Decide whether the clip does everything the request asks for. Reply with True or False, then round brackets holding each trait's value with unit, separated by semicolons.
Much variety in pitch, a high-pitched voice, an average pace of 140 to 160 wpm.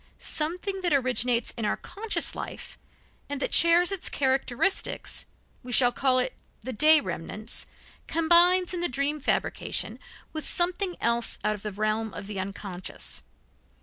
True (7.6 semitones; 270 Hz; 145 wpm)